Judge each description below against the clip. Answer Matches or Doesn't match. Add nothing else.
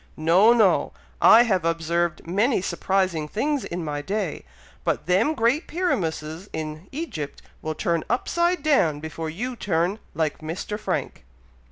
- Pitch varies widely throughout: Matches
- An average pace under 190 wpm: Matches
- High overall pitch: Doesn't match